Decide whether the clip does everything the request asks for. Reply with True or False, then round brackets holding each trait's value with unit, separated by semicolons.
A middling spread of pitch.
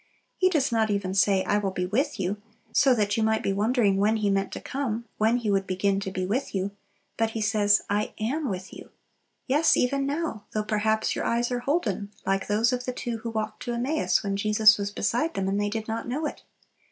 True (3.3 semitones)